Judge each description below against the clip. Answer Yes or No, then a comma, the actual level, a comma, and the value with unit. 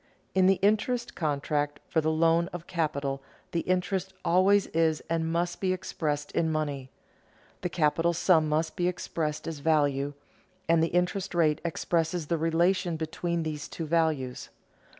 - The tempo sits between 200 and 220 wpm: No, average, 155 wpm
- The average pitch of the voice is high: No, medium, 165 Hz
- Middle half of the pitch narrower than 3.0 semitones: Yes, narrow, 2.5 semitones